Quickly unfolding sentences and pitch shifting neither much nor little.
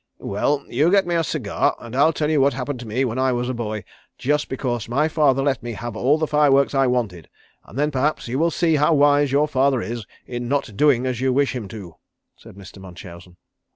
Yes: fast, 235 wpm; average, 3.8 semitones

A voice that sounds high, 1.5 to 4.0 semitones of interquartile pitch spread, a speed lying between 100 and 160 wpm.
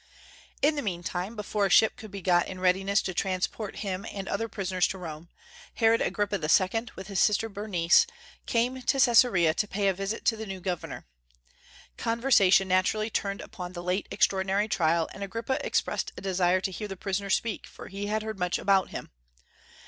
No: high, 195 Hz; average, 2.8 semitones; average, 185 wpm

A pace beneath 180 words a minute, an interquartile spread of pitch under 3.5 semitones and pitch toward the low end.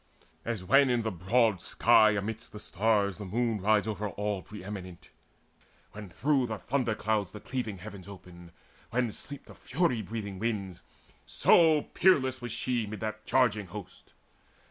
Yes: average, 155 wpm; average, 3.1 semitones; low, 110 Hz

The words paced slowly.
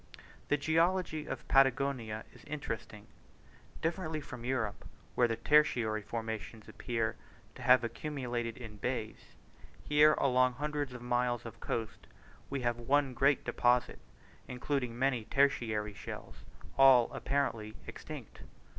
Yes: slow, 120 wpm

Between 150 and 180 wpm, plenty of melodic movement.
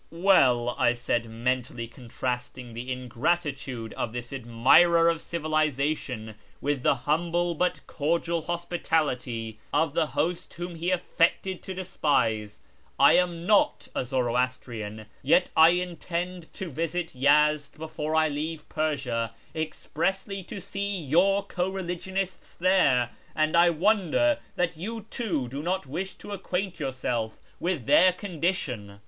No: slow, 135 wpm; wide, 5.7 semitones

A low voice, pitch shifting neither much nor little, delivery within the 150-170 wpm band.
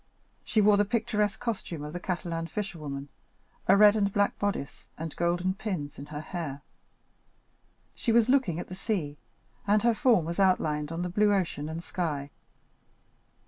No: medium, 180 Hz; average, 4.8 semitones; average, 165 wpm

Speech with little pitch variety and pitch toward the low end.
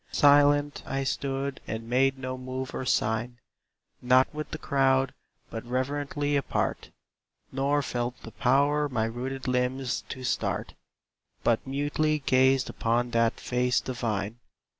Yes: narrow, 2.2 semitones; low, 130 Hz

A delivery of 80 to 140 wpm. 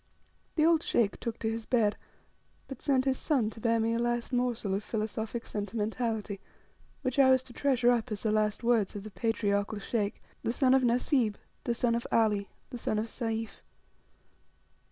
No: average, 185 wpm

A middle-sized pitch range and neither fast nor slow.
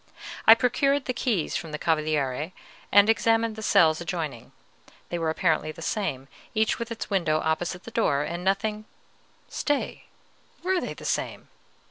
No: wide, 6.1 semitones; average, 155 wpm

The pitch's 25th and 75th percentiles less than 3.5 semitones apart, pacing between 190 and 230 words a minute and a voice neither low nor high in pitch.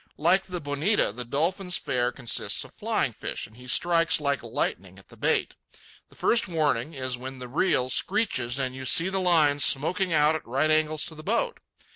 No: average, 5.1 semitones; average, 195 wpm; medium, 150 Hz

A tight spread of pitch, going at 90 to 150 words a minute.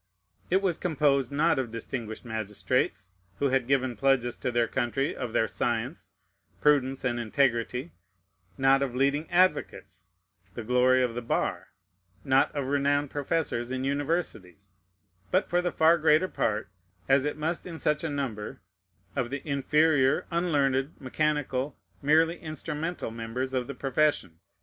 No: average, 3.8 semitones; average, 145 wpm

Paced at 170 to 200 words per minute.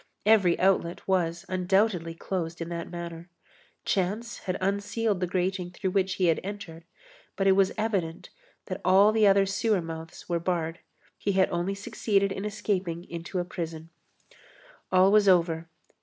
No: average, 155 wpm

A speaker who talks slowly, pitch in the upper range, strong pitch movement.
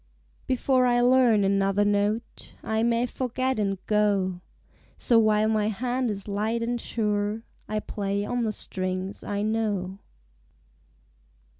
No: slow, 130 wpm; high, 215 Hz; narrow, 2.6 semitones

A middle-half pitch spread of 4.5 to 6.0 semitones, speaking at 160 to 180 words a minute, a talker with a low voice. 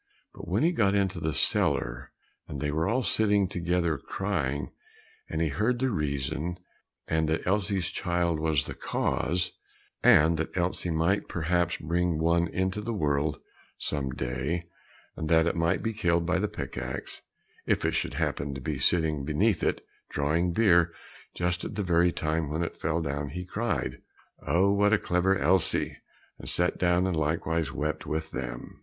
No: average, 3.2 semitones; average, 175 wpm; very low, 85 Hz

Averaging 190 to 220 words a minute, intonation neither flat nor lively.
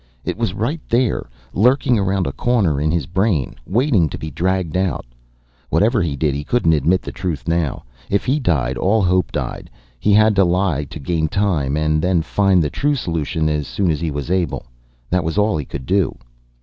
Yes: average, 200 wpm; average, 4.6 semitones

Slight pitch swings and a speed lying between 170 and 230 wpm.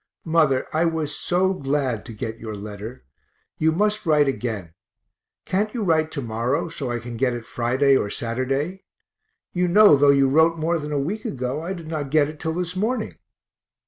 No: average, 5.1 semitones; average, 190 wpm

